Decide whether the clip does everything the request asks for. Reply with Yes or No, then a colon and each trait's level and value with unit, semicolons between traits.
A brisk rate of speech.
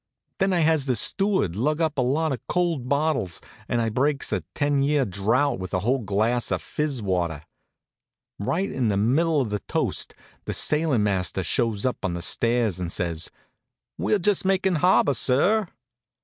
No: average, 180 wpm